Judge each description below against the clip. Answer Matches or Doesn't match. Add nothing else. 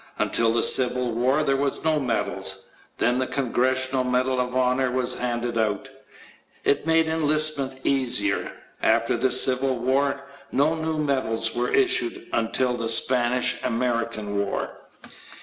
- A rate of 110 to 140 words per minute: Matches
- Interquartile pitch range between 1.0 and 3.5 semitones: Matches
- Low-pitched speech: Matches